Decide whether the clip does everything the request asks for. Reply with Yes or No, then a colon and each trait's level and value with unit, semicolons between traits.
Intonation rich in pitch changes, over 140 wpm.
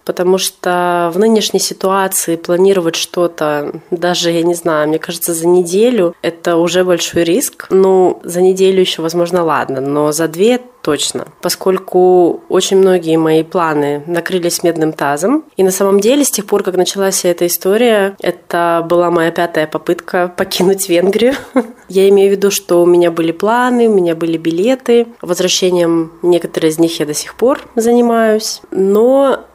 No: narrow, 2.5 semitones; fast, 160 wpm